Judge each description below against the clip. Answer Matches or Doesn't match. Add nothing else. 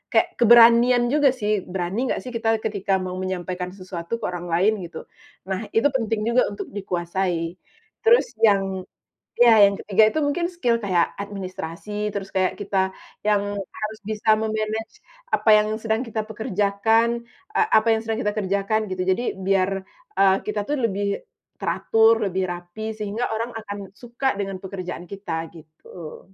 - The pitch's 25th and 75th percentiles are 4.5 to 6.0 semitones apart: Doesn't match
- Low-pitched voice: Doesn't match